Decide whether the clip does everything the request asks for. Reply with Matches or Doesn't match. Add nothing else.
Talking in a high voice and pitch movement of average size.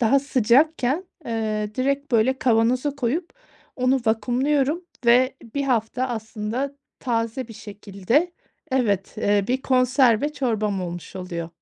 Matches